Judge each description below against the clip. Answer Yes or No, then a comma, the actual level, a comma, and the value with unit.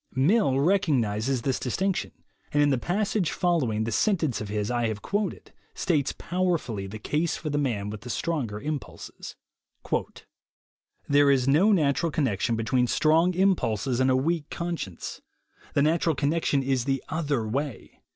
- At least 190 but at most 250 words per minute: No, average, 150 wpm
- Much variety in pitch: Yes, wide, 5.9 semitones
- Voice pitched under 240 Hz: Yes, medium, 140 Hz